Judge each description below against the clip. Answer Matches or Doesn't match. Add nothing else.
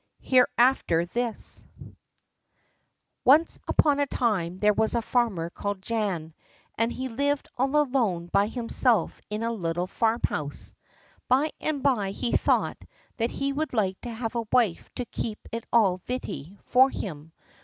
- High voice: Matches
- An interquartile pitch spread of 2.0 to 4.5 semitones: Doesn't match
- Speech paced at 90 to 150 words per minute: Matches